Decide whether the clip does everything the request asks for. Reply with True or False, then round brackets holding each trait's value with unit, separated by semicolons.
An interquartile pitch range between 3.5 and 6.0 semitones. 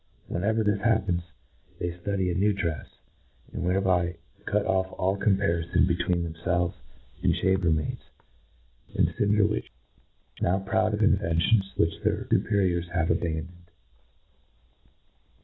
False (2.5 semitones)